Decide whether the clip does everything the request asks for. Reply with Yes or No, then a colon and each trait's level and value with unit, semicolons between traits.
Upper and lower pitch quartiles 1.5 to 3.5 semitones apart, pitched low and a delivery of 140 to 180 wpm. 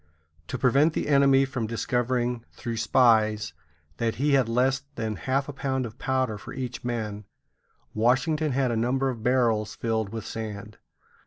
Yes: average, 3.0 semitones; low, 120 Hz; average, 160 wpm